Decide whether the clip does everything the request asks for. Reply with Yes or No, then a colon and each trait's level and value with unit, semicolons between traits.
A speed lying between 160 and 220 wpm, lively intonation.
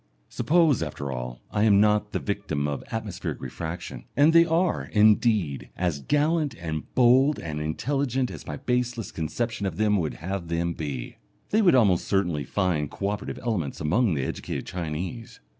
Yes: average, 165 wpm; wide, 7.6 semitones